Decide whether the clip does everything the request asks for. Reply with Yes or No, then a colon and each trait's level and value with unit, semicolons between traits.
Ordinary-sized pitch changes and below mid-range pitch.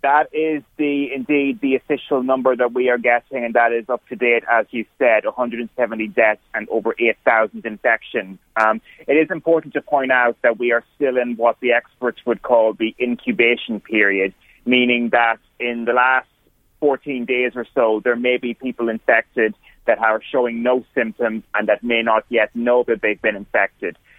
No: narrow, 2.0 semitones; low, 120 Hz